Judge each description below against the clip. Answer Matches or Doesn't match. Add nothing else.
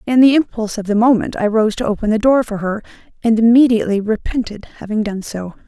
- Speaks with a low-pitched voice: Doesn't match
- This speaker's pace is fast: Matches